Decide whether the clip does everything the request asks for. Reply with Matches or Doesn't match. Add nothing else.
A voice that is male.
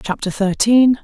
Doesn't match